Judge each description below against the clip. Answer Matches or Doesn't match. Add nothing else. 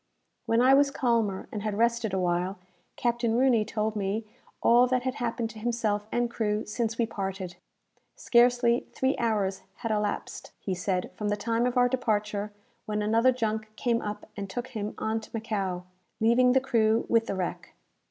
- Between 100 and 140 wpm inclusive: Doesn't match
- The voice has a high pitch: Matches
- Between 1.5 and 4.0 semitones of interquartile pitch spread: Matches